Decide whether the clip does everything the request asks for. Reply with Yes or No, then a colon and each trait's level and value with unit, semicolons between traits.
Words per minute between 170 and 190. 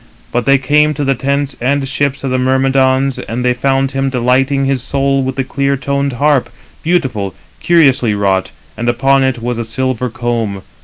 Yes: average, 185 wpm